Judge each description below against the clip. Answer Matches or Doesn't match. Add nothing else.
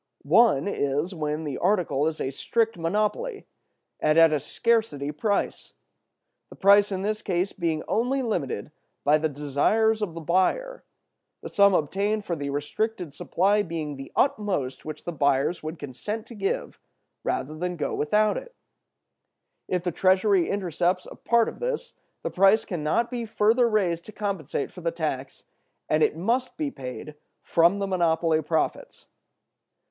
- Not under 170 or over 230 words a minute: Doesn't match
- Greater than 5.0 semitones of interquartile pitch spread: Matches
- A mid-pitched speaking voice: Matches